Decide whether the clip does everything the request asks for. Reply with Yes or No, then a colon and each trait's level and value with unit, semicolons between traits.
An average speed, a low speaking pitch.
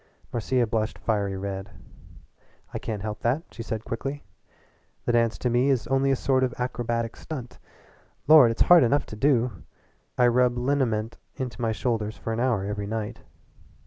Yes: average, 170 wpm; low, 120 Hz